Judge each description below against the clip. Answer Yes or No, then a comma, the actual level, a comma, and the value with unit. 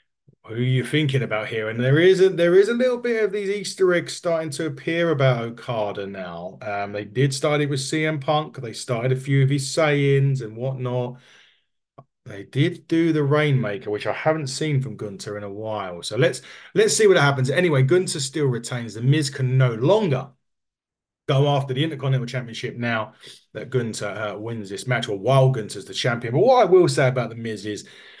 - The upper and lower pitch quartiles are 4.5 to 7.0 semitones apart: Yes, average, 5.3 semitones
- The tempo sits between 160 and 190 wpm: No, fast, 205 wpm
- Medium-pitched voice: No, low, 130 Hz